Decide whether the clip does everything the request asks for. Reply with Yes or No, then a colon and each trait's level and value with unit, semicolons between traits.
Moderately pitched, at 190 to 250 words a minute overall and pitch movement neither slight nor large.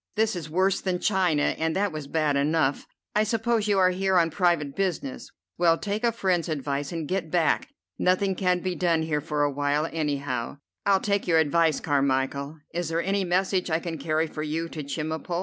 Yes: medium, 165 Hz; average, 200 wpm; average, 3.8 semitones